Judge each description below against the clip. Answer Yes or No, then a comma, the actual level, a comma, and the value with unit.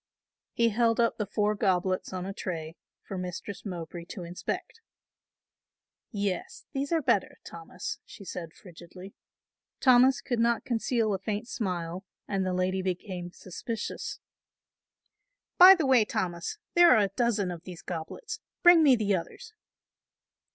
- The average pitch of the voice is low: No, high, 200 Hz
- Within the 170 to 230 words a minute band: No, average, 145 wpm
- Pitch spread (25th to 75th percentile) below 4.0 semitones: No, average, 4.6 semitones